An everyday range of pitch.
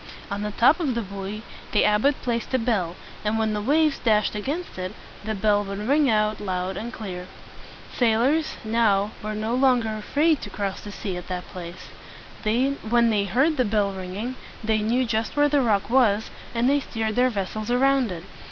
Yes: average, 3.6 semitones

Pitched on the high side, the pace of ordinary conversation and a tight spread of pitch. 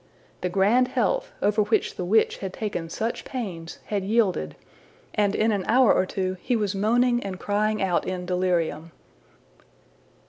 No: high, 200 Hz; average, 160 wpm; average, 3.2 semitones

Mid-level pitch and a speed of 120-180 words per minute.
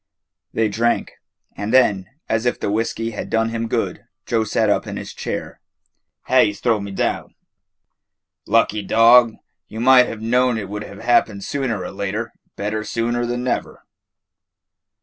No: low, 115 Hz; average, 160 wpm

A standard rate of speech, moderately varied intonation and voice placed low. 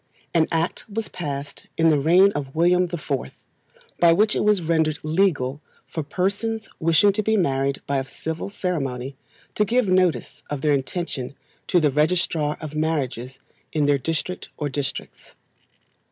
No: average, 160 wpm; average, 4.4 semitones; medium, 160 Hz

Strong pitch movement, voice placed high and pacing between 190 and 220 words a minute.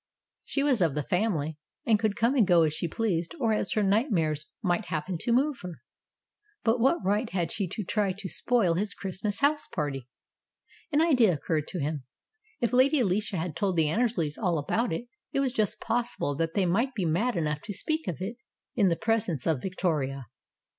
Yes: wide, 5.9 semitones; high, 195 Hz; average, 200 wpm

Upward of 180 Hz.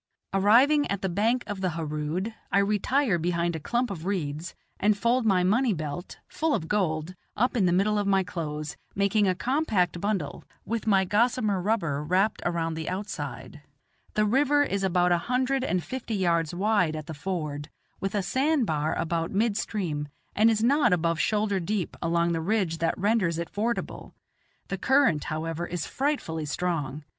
Yes: high, 190 Hz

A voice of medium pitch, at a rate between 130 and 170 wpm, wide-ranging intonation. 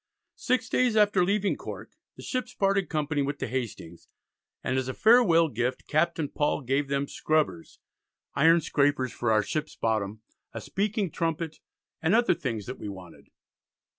Yes: medium, 150 Hz; average, 160 wpm; wide, 7.1 semitones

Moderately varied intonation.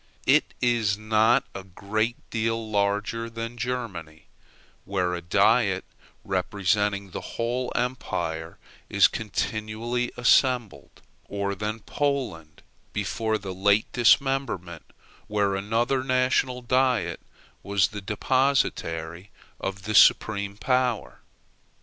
Yes: average, 3.7 semitones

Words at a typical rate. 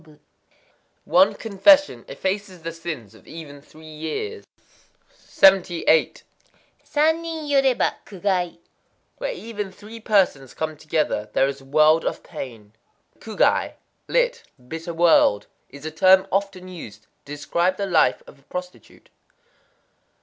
No: slow, 125 wpm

